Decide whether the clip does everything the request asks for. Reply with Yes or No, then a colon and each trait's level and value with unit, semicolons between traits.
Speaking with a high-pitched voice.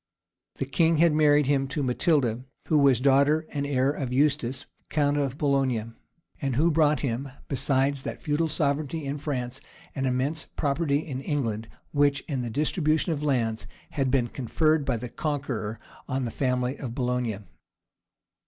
No: medium, 140 Hz